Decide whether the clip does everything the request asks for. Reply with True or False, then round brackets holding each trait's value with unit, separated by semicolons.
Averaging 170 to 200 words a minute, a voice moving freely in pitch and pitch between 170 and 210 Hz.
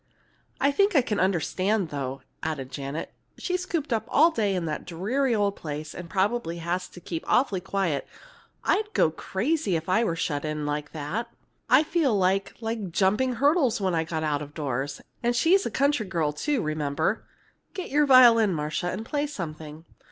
True (180 wpm; 8.0 semitones; 190 Hz)